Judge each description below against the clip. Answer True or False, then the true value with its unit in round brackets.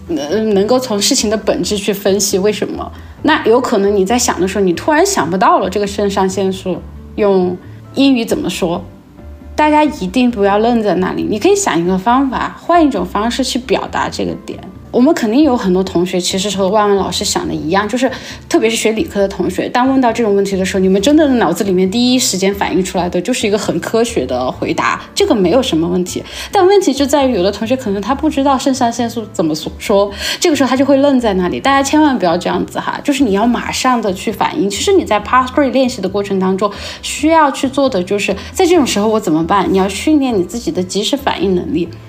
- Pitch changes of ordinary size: False (5.9 semitones)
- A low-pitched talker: False (220 Hz)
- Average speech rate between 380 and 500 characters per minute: False (360 characters per minute)